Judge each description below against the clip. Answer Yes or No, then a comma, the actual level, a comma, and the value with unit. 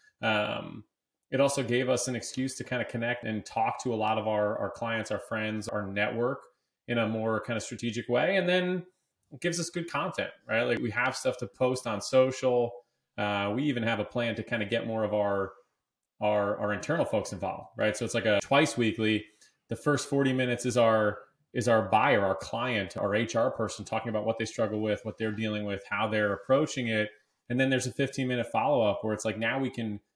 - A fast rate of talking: Yes, fast, 225 wpm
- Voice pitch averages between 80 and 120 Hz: Yes, low, 115 Hz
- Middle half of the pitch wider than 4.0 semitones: No, average, 3.1 semitones